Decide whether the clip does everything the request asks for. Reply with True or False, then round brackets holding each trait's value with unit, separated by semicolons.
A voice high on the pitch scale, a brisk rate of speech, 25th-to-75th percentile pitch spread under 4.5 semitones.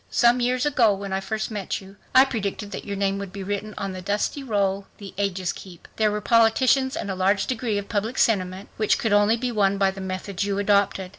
True (205 Hz; 230 wpm; 2.4 semitones)